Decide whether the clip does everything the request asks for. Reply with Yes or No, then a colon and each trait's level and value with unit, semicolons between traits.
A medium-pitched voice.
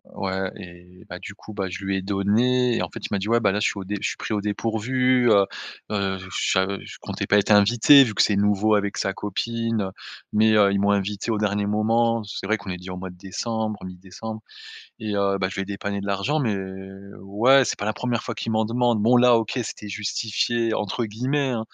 No: low, 105 Hz